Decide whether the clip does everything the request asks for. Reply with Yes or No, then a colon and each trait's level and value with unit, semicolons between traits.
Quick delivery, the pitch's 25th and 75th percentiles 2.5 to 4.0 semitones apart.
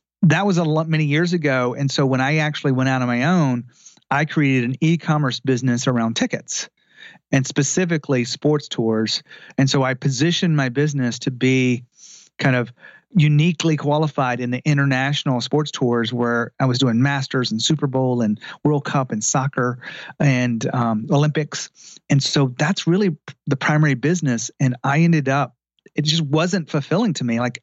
No: average, 170 wpm; average, 3.4 semitones